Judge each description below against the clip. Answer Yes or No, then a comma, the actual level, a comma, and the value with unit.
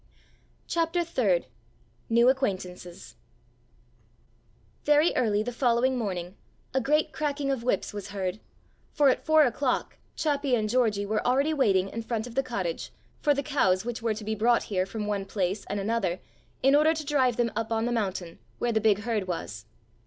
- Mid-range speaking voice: No, high, 230 Hz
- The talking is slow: No, average, 175 wpm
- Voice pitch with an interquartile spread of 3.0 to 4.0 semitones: No, average, 5.0 semitones